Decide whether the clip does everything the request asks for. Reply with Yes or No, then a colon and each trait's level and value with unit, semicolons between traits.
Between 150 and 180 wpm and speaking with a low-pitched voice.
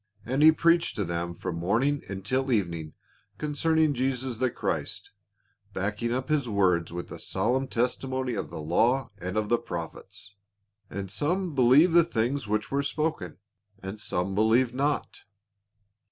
Yes: average, 155 wpm; low, 120 Hz